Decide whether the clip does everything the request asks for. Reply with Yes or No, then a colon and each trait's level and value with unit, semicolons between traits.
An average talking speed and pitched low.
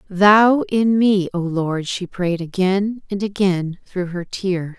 No: average, 165 wpm; high, 190 Hz